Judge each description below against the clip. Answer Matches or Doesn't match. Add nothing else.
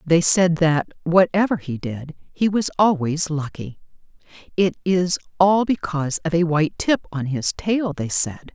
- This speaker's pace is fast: Doesn't match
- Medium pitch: Matches